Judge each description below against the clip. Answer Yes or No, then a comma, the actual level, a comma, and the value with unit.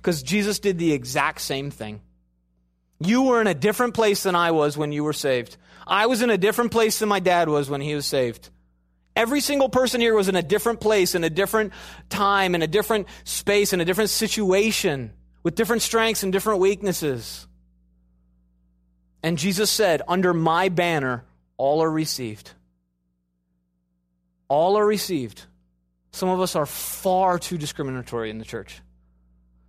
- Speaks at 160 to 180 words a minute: Yes, average, 170 wpm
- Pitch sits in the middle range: Yes, medium, 160 Hz